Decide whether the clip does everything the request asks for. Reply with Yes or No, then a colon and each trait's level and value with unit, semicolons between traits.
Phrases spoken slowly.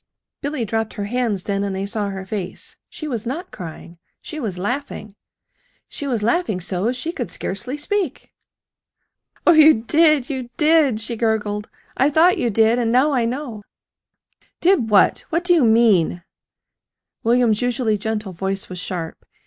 No: average, 160 wpm